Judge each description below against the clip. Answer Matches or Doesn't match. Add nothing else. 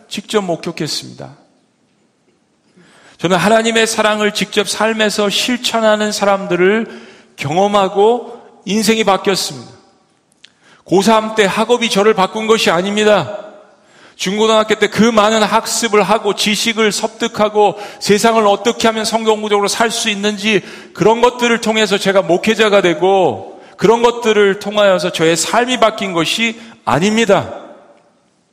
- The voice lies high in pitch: Matches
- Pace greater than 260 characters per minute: Matches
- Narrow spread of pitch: Matches